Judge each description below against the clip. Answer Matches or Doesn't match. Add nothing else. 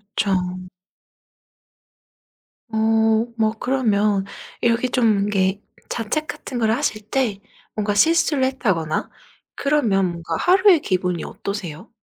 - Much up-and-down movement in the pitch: Doesn't match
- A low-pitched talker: Doesn't match